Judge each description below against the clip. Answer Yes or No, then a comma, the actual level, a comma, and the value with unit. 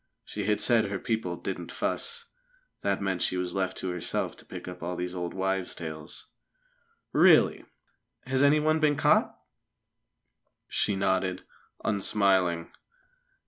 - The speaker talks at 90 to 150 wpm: Yes, slow, 135 wpm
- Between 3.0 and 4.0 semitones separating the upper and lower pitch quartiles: Yes, average, 3.3 semitones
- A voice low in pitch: Yes, very low, 95 Hz